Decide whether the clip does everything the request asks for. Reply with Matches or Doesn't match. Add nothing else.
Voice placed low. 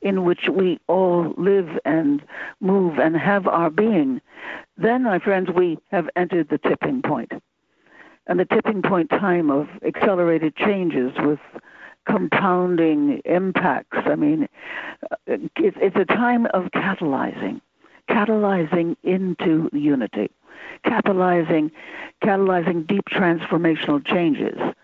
Doesn't match